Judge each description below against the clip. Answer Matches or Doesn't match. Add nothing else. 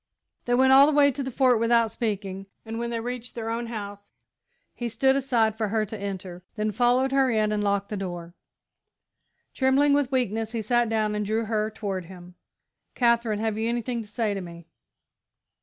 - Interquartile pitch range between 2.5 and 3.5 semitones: Matches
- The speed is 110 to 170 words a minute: Doesn't match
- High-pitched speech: Matches